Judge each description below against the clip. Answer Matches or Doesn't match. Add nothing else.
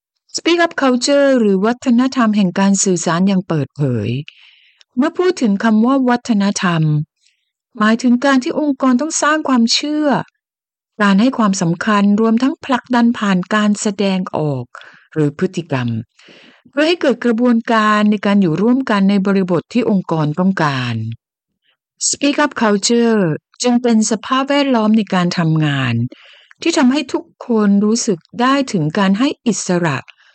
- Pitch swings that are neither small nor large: Doesn't match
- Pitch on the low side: Doesn't match